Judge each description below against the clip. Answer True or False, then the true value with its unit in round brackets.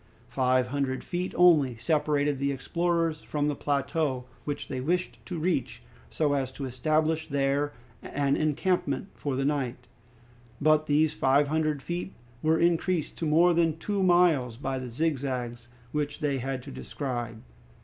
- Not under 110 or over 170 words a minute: True (150 wpm)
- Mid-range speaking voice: True (145 Hz)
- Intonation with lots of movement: False (3.3 semitones)